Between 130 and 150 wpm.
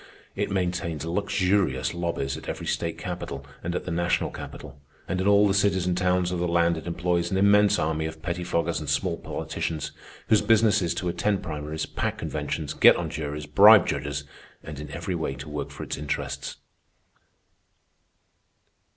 No: average, 175 wpm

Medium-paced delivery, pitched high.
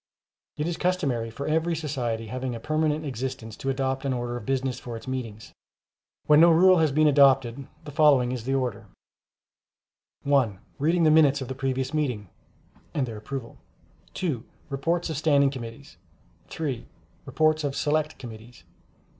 No: average, 160 wpm; low, 135 Hz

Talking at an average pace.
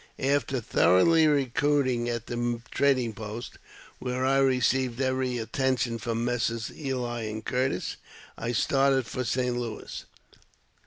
No: slow, 125 wpm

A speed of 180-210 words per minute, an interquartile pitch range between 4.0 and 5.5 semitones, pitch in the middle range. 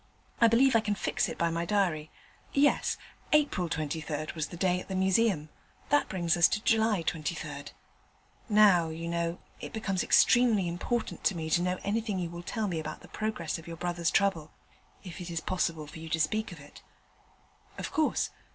Yes: average, 190 wpm; average, 4.4 semitones; medium, 175 Hz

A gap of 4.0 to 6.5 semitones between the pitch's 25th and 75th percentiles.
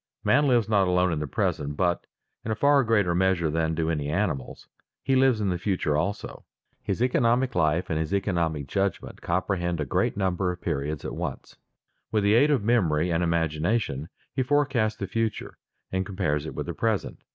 Yes: average, 5.3 semitones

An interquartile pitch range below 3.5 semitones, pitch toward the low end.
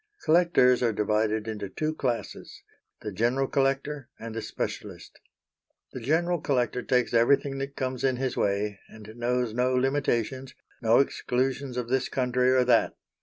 Yes: average, 2.8 semitones; low, 125 Hz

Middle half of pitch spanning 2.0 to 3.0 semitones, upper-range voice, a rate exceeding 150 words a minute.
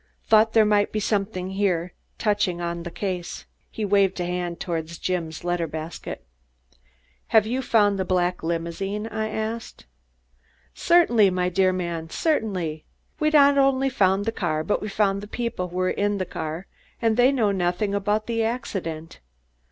No: average, 3.7 semitones; high, 195 Hz; average, 165 wpm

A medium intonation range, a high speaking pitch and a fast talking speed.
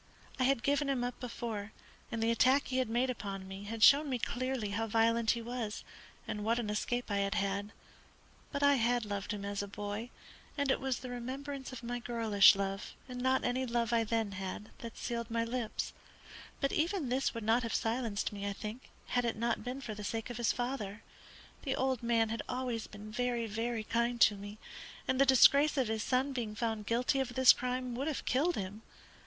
Yes: average, 3.1 semitones; high, 235 Hz; fast, 210 wpm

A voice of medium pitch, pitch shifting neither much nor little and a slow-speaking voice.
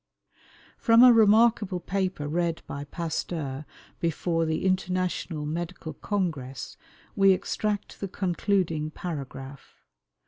Yes: medium, 175 Hz; average, 4.2 semitones; slow, 100 wpm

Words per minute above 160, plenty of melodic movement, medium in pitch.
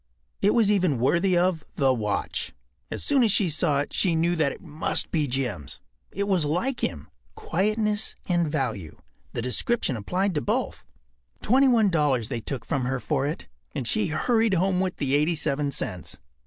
Yes: average, 175 wpm; wide, 6.5 semitones; medium, 160 Hz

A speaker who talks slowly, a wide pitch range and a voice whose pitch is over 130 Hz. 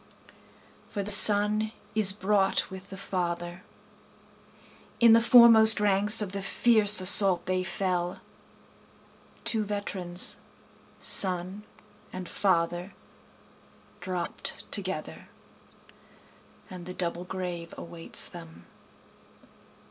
No: slow, 95 wpm; average, 2.7 semitones; high, 190 Hz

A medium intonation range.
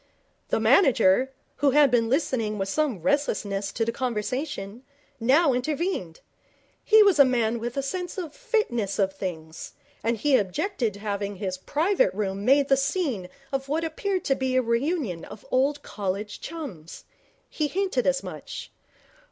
No: wide, 6.8 semitones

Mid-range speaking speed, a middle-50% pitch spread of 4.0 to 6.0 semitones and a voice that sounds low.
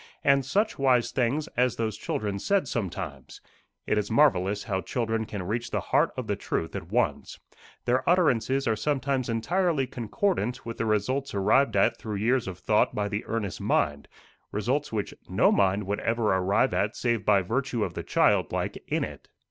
Yes: average, 180 wpm; average, 4.4 semitones; low, 115 Hz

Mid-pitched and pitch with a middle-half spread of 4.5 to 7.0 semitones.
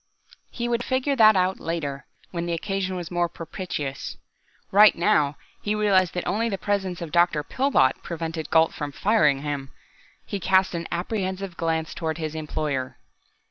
No: medium, 175 Hz; average, 3.8 semitones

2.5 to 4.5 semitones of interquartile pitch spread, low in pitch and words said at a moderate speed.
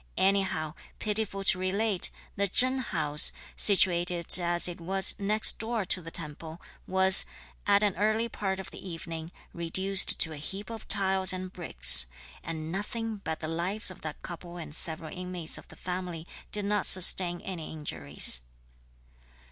No: average, 3.2 semitones; medium, 185 Hz; average, 155 wpm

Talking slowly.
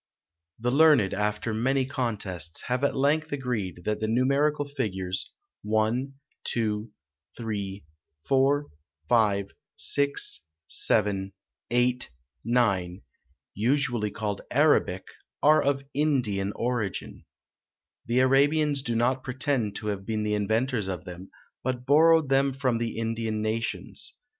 Yes: slow, 120 wpm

